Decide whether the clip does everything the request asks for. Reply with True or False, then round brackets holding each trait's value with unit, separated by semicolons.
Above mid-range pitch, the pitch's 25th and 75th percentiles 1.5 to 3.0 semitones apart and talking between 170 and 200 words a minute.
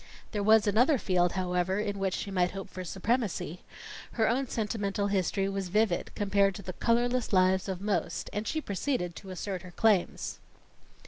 True (200 Hz; 2.7 semitones; 175 wpm)